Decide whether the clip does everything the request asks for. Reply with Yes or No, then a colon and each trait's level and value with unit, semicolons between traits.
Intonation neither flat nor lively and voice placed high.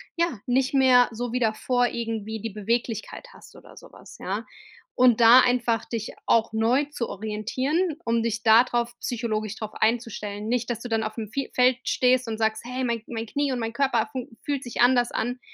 No: narrow, 2.2 semitones; high, 235 Hz